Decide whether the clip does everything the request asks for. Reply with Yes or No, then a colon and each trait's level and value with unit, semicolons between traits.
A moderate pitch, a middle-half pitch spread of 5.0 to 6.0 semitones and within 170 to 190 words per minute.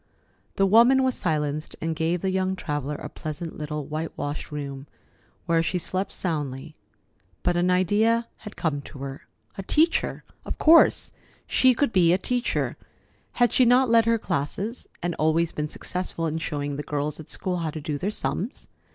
Yes: medium, 170 Hz; wide, 5.6 semitones; average, 175 wpm